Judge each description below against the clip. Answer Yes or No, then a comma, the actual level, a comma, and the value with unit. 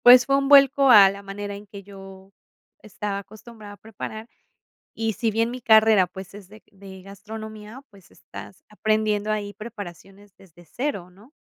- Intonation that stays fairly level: Yes, narrow, 2.1 semitones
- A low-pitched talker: No, high, 210 Hz